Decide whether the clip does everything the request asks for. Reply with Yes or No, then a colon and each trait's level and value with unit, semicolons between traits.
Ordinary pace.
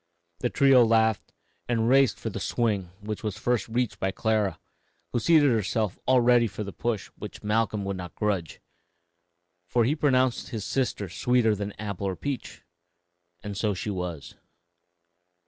Yes: average, 160 wpm